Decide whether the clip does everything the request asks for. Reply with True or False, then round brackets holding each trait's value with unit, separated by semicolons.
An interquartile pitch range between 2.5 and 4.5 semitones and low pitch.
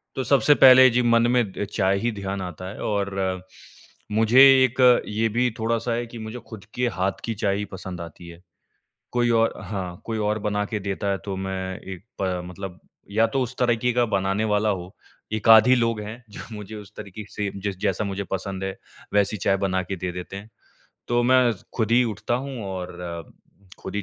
True (3.4 semitones; 105 Hz)